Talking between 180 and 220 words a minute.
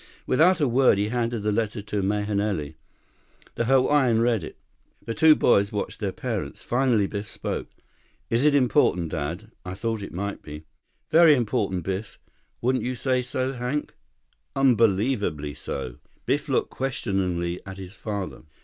No: average, 150 wpm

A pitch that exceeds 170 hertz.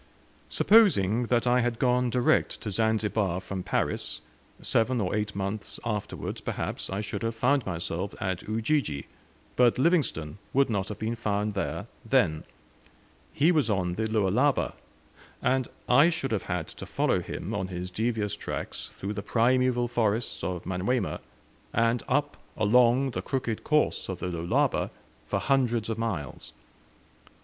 No: low, 110 Hz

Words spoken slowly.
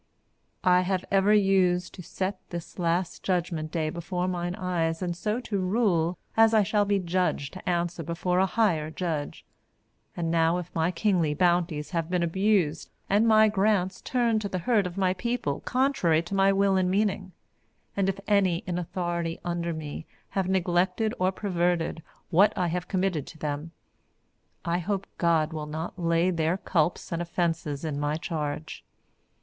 No: average, 170 wpm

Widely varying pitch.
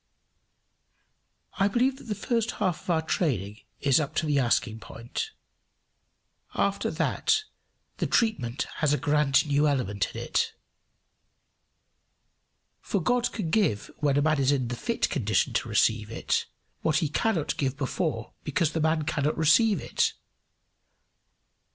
Yes: wide, 6.0 semitones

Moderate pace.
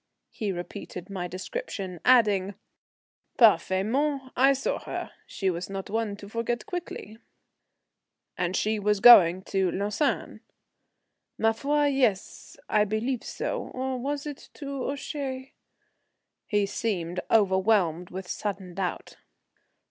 No: slow, 120 wpm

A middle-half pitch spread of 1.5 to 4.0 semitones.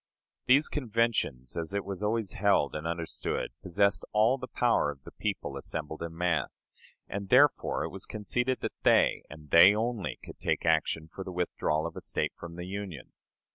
No: average, 5.1 semitones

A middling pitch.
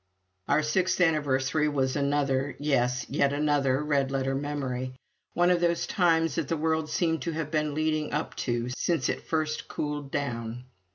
Yes: medium, 145 Hz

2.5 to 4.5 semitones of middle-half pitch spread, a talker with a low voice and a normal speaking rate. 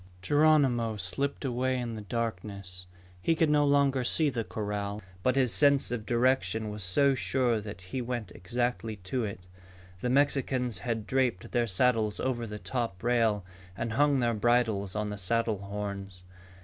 Yes: average, 3.8 semitones; low, 115 Hz; average, 160 wpm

